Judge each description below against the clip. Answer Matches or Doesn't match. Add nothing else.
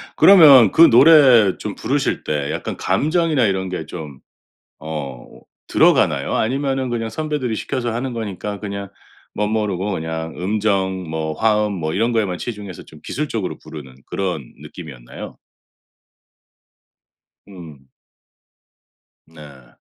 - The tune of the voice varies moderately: Doesn't match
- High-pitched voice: Doesn't match